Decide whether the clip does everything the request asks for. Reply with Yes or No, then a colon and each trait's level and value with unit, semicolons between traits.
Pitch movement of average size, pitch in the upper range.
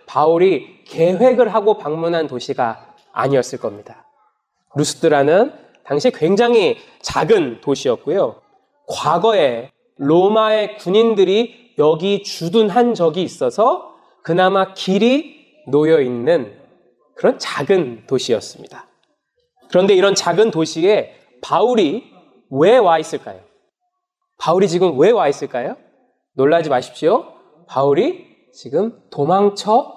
No: wide, 7.1 semitones; high, 200 Hz